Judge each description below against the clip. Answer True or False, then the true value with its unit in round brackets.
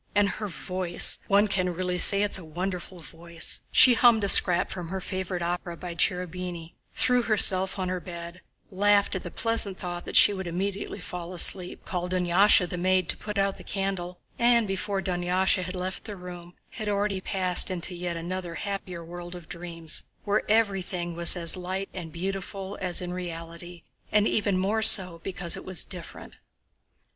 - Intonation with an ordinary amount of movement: False (2.0 semitones)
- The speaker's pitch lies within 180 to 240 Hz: True (185 Hz)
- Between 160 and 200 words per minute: True (180 wpm)